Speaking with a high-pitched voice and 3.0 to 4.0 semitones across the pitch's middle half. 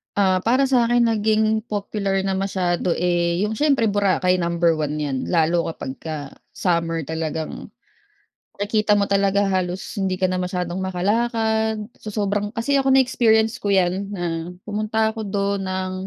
Yes: high, 195 Hz; average, 3.7 semitones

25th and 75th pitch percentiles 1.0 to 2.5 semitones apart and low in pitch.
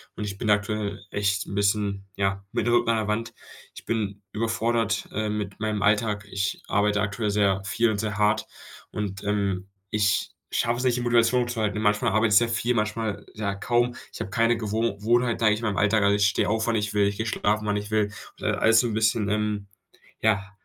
Yes: narrow, 1.8 semitones; low, 105 Hz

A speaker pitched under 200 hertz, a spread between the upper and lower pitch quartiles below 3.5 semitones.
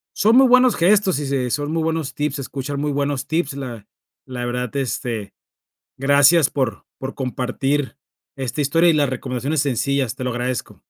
Yes: medium, 140 Hz; average, 3.0 semitones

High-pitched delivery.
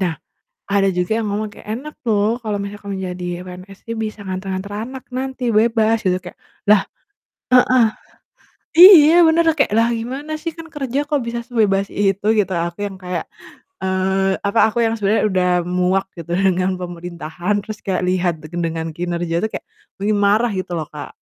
Yes: high, 200 Hz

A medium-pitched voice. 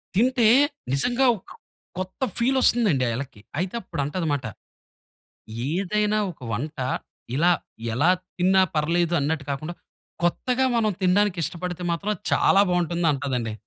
Yes: medium, 175 Hz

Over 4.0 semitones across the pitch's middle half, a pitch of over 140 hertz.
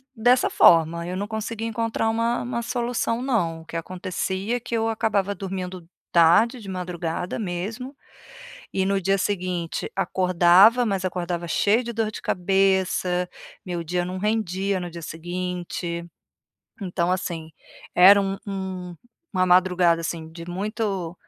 No: average, 3.4 semitones; medium, 185 Hz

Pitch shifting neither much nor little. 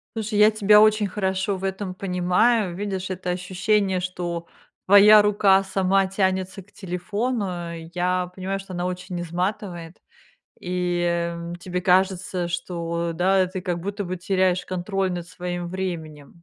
No: narrow, 1.7 semitones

